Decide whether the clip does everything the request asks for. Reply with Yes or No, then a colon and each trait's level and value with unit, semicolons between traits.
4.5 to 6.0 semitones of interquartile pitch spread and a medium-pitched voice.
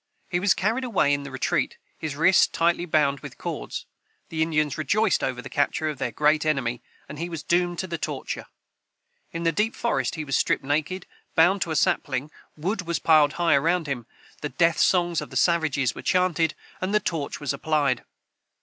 No: average, 3.3 semitones; medium, 160 Hz